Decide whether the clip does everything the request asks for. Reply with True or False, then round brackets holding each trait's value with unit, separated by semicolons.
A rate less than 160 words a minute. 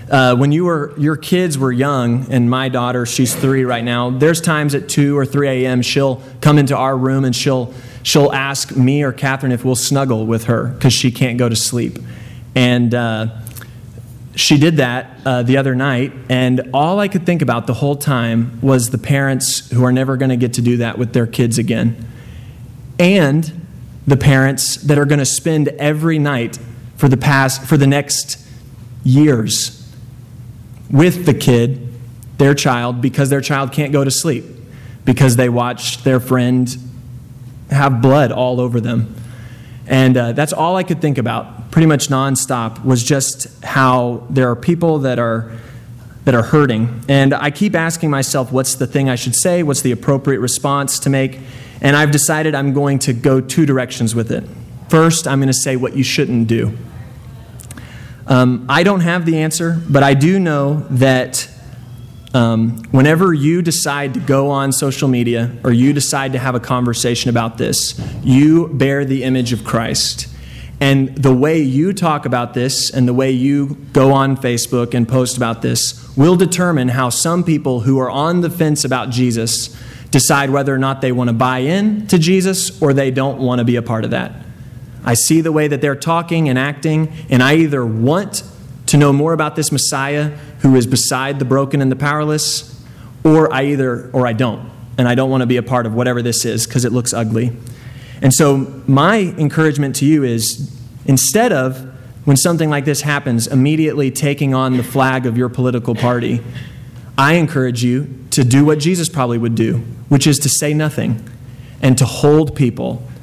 False (190 wpm)